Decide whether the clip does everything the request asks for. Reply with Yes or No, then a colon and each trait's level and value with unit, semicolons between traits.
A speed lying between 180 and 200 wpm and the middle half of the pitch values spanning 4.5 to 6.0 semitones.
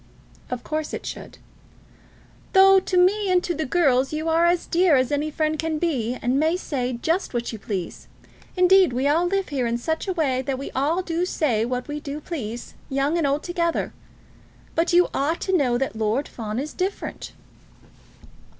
Yes: average, 195 wpm; average, 5.3 semitones